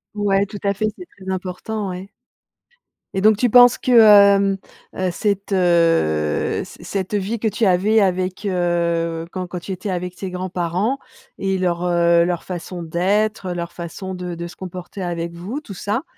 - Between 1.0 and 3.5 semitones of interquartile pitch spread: Yes, average, 2.7 semitones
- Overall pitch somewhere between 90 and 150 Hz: No, medium, 185 Hz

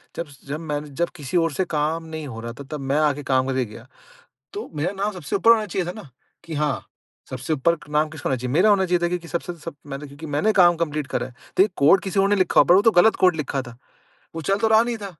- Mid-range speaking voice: Yes, medium, 160 Hz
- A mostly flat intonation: No, average, 4.4 semitones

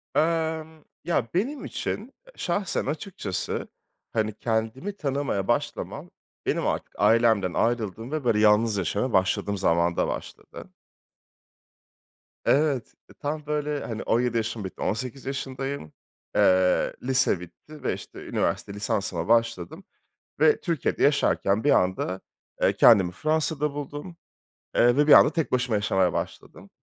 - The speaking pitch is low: Yes, low, 125 Hz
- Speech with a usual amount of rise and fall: No, wide, 6.3 semitones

